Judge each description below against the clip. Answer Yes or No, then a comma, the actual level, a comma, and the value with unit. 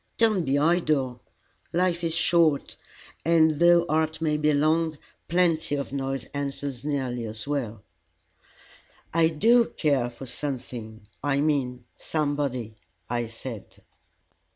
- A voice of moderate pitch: Yes, medium, 145 Hz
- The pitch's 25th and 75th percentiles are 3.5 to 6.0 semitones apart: Yes, average, 4.1 semitones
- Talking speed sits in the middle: No, slow, 120 wpm